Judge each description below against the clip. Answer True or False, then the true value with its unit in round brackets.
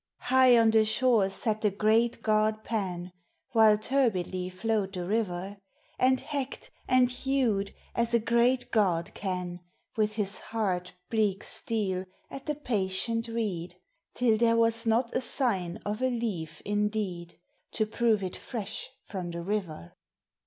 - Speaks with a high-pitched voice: True (215 Hz)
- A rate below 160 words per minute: True (145 wpm)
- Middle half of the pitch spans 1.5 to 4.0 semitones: True (3.6 semitones)